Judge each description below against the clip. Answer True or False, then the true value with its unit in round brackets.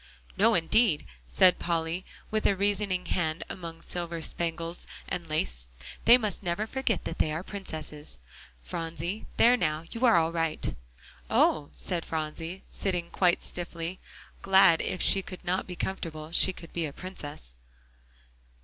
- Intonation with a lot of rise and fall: False (2.9 semitones)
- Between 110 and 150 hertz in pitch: False (170 Hz)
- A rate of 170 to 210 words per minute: False (150 wpm)